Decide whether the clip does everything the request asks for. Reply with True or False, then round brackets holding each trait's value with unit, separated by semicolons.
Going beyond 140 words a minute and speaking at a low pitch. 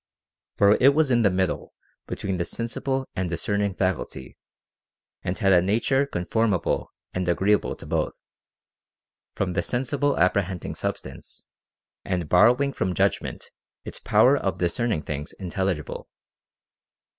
False (135 wpm; 95 Hz)